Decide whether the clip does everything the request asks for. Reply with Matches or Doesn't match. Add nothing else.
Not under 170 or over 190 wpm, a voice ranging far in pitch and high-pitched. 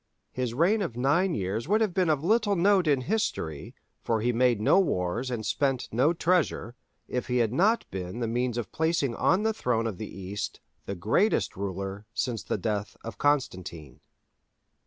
Doesn't match